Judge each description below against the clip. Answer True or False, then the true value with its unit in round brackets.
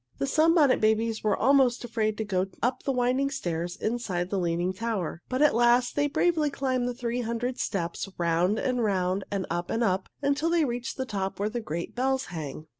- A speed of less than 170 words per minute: False (200 wpm)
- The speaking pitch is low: False (230 Hz)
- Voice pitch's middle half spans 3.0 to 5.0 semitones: False (5.4 semitones)